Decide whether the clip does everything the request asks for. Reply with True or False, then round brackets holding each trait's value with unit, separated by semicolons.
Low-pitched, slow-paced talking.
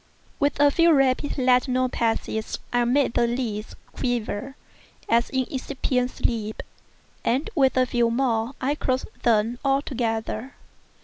False (250 Hz; 130 wpm)